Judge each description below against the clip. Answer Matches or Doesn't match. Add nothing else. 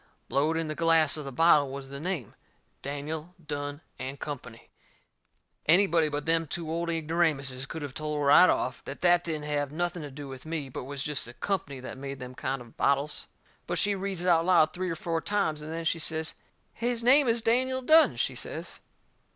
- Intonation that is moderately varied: Matches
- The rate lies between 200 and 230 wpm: Matches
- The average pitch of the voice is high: Doesn't match